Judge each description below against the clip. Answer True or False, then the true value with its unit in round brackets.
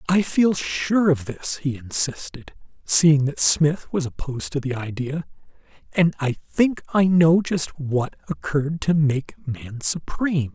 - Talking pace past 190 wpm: False (155 wpm)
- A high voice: False (150 Hz)